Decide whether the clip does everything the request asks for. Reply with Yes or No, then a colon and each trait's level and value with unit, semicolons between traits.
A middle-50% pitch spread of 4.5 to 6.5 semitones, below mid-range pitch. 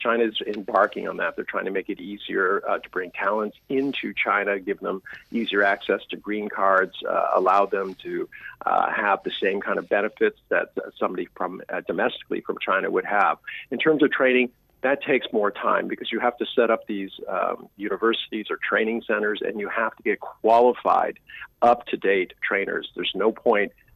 Yes: average, 5.2 semitones; low, 115 Hz